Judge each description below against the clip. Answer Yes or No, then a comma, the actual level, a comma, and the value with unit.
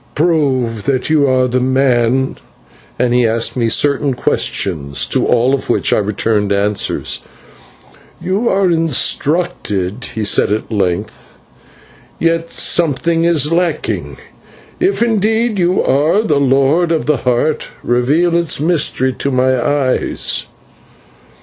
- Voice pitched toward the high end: No, low, 135 Hz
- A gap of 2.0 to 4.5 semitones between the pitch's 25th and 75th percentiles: No, wide, 5.6 semitones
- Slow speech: Yes, slow, 130 wpm